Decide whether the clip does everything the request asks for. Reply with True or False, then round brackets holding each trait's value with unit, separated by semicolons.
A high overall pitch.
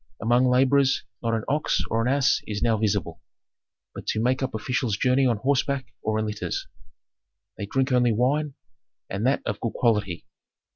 False (120 Hz)